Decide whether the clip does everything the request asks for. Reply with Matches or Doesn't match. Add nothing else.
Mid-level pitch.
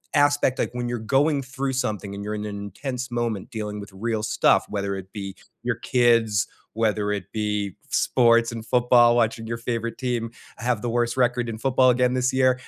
Doesn't match